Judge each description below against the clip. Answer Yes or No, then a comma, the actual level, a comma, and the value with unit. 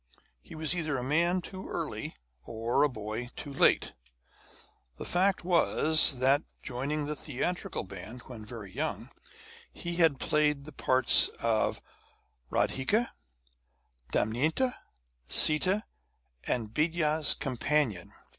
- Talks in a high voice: No, medium, 145 Hz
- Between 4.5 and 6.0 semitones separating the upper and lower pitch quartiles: Yes, average, 4.9 semitones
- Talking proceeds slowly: Yes, slow, 115 wpm